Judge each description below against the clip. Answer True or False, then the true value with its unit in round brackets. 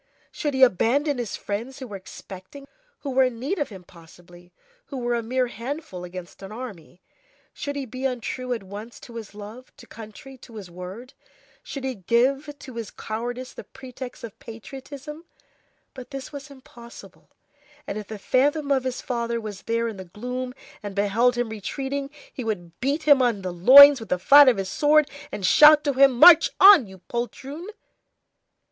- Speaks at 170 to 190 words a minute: True (185 wpm)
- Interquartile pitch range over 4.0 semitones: True (4.7 semitones)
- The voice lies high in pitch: True (245 Hz)